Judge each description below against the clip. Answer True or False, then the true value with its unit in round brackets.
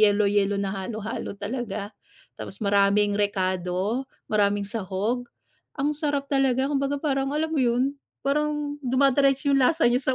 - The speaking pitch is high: True (245 Hz)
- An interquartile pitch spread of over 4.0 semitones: True (5.3 semitones)